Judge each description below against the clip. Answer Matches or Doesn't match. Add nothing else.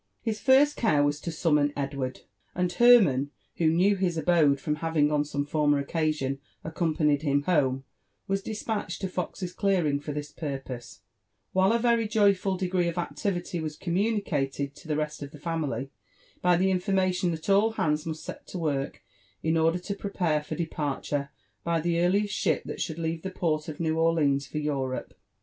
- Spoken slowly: Doesn't match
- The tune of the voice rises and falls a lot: Doesn't match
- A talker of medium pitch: Matches